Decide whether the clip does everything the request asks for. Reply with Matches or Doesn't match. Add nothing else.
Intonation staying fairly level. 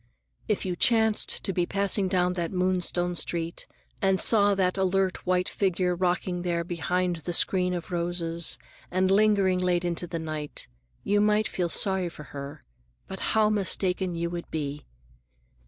Matches